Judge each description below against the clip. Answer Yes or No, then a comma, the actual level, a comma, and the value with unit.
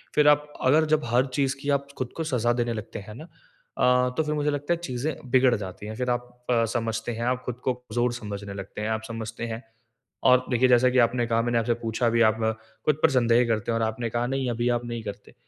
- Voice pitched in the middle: No, low, 120 Hz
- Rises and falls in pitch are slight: Yes, narrow, 2.1 semitones